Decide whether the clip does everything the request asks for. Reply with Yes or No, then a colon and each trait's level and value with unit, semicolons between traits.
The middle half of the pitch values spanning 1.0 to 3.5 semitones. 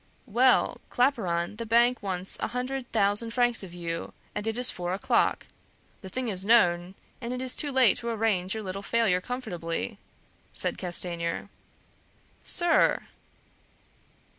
No: average, 5.1 semitones